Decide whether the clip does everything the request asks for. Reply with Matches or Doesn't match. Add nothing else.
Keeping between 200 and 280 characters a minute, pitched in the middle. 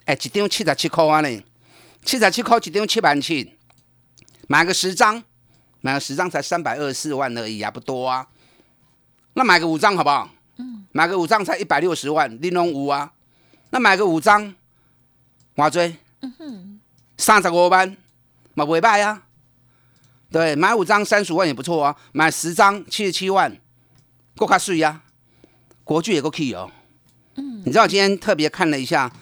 Matches